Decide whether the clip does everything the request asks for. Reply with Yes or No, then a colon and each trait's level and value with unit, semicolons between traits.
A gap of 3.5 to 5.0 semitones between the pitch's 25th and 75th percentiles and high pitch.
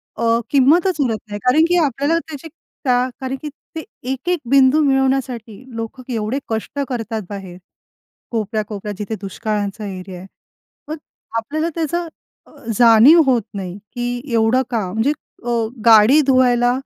Yes: average, 4.2 semitones; high, 245 Hz